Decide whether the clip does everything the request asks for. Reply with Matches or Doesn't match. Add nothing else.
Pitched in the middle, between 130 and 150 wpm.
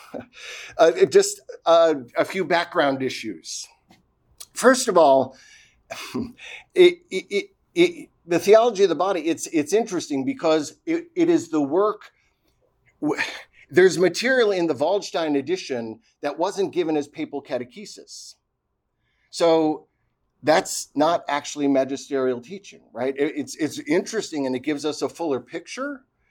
Matches